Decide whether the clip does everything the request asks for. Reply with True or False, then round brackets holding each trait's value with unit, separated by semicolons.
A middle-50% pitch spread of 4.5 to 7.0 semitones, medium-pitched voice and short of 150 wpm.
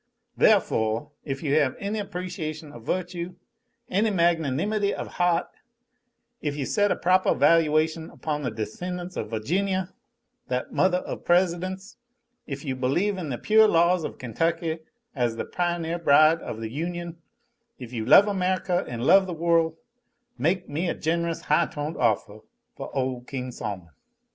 False (4.9 semitones; 165 Hz; 155 wpm)